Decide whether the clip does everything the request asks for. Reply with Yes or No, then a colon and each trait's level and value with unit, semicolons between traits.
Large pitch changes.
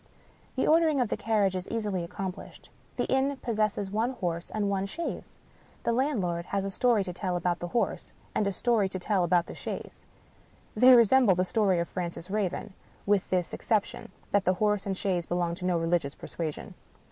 No: average, 3.6 semitones